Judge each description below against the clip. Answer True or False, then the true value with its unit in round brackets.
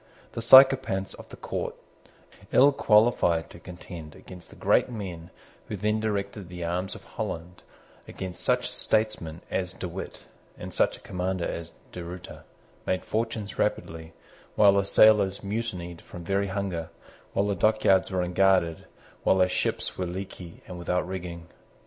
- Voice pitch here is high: False (95 Hz)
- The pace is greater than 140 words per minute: True (155 wpm)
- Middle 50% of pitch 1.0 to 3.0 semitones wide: True (2.6 semitones)